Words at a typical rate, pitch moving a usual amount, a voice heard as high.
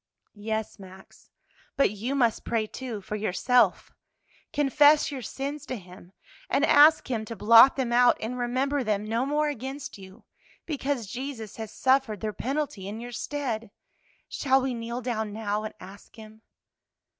Yes: average, 155 wpm; average, 3.8 semitones; high, 235 Hz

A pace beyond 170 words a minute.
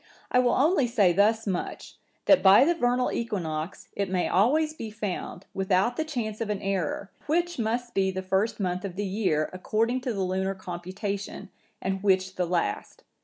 Yes: average, 180 wpm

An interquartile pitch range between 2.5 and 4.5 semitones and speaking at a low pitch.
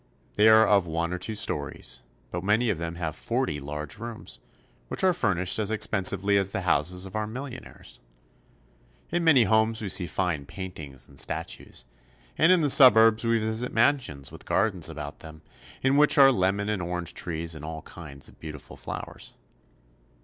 No: average, 5.3 semitones; very low, 95 Hz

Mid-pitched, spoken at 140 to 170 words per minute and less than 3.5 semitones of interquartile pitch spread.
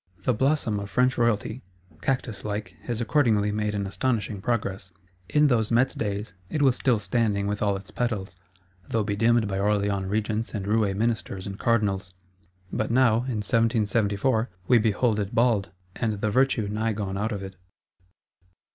No: low, 105 Hz; average, 165 wpm; narrow, 2.6 semitones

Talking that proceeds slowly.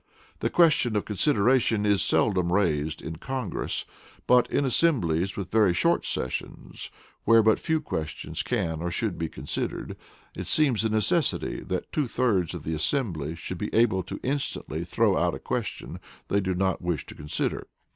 No: average, 165 wpm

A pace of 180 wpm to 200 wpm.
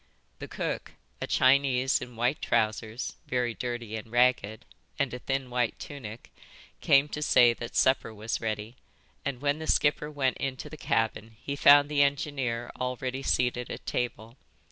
No: average, 160 wpm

